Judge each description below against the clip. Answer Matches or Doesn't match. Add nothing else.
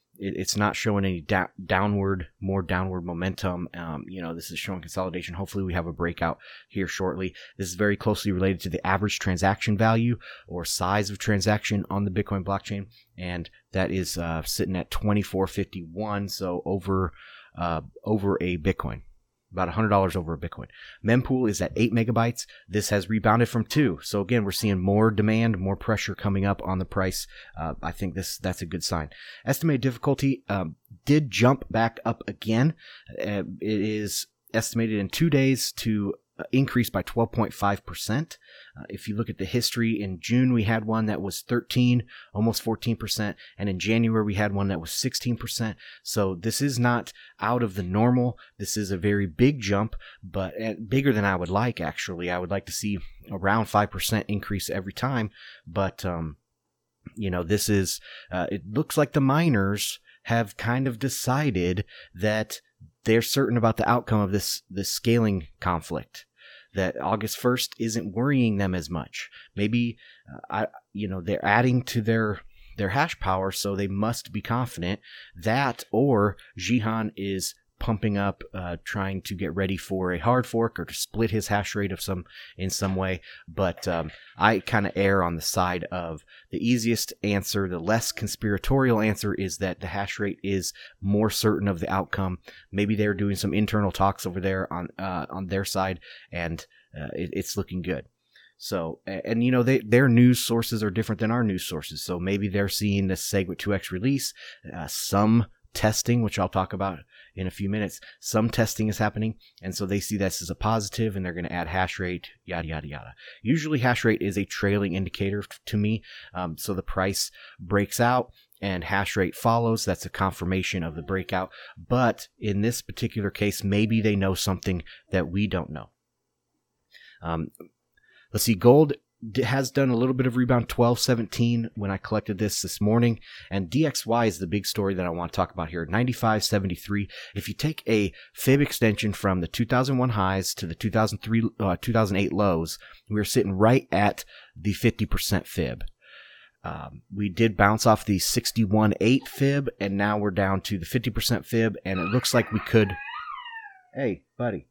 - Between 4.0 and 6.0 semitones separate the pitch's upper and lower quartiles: Doesn't match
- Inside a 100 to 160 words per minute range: Doesn't match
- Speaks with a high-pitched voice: Doesn't match